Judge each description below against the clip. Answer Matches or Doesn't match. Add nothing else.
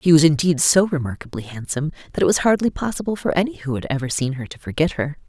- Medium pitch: Matches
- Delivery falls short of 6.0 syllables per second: Doesn't match